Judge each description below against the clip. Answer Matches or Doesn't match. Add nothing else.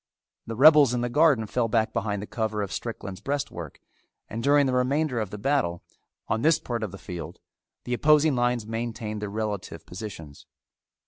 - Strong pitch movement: Doesn't match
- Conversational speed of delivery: Matches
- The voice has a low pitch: Matches